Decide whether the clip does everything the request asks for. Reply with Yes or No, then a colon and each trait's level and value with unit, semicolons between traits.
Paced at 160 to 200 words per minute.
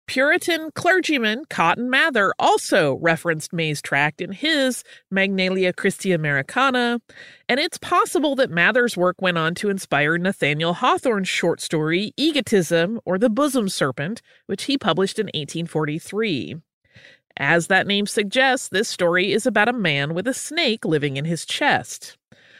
No: average, 145 wpm